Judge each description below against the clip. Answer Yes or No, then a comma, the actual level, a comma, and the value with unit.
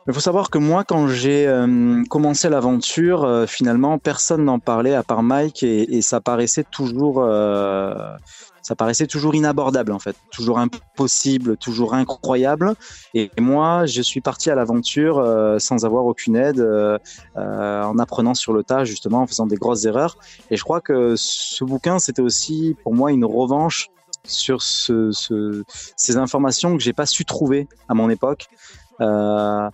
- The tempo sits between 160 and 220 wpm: Yes, average, 170 wpm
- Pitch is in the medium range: No, low, 130 Hz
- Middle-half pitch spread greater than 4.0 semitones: Yes, average, 4.6 semitones